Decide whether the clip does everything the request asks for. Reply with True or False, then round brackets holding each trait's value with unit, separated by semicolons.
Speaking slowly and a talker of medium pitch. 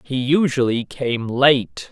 False (125 wpm; 130 Hz)